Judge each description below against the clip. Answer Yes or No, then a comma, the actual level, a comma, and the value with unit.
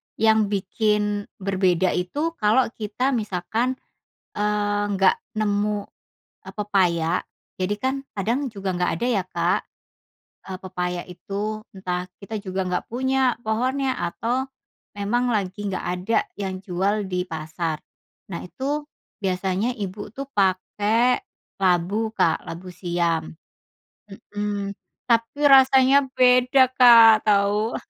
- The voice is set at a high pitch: Yes, high, 205 Hz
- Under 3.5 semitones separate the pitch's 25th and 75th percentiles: No, average, 3.8 semitones